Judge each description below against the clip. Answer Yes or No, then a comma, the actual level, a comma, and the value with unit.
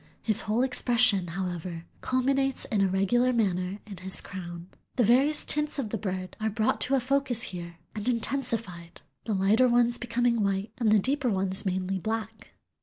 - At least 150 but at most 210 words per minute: Yes, average, 175 wpm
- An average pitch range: Yes, average, 4.5 semitones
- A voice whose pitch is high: Yes, high, 215 Hz